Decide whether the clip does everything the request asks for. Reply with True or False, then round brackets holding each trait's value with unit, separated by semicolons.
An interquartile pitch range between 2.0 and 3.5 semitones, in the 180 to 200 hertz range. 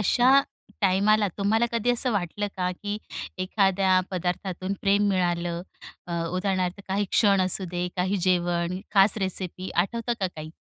True (2.4 semitones; 190 Hz)